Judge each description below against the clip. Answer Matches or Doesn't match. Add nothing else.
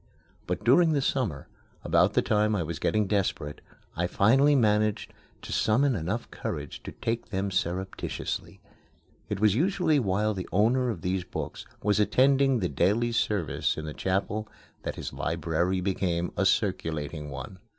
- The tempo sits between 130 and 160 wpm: Matches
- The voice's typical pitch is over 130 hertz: Doesn't match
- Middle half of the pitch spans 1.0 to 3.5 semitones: Doesn't match